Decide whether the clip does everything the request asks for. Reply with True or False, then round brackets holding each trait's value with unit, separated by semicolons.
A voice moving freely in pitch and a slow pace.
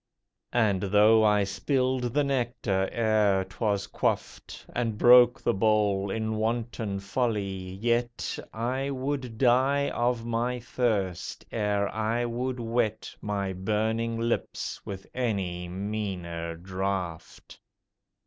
False (3.5 semitones; 110 wpm)